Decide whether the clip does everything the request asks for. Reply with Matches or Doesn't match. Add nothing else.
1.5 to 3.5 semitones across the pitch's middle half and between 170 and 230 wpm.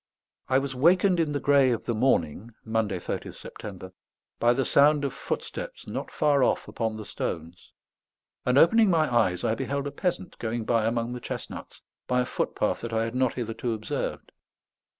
Doesn't match